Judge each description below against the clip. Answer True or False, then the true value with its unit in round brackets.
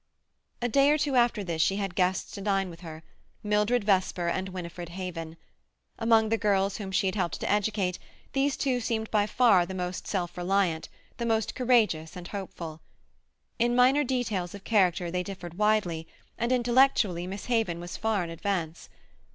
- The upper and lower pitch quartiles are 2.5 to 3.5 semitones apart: False (4.2 semitones)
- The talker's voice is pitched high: True (195 Hz)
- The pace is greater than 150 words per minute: True (175 wpm)